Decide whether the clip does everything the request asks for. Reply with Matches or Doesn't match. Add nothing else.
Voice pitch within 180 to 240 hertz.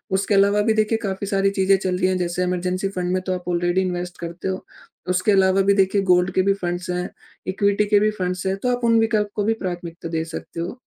Matches